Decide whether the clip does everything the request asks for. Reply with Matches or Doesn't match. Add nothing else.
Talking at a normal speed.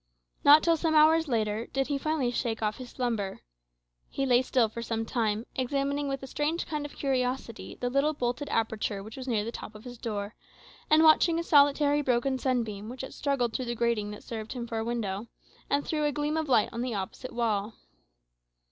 Doesn't match